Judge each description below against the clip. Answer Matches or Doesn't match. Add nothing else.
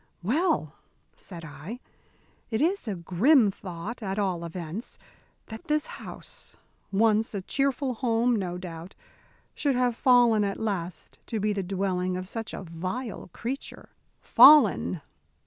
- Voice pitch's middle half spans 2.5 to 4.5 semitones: Doesn't match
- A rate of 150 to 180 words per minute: Doesn't match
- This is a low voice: Doesn't match